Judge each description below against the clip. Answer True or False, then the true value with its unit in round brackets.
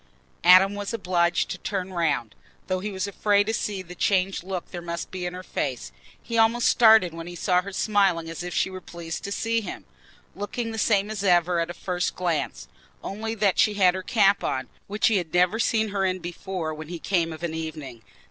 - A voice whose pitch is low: False (185 Hz)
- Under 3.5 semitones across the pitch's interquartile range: True (2.9 semitones)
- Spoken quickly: True (215 wpm)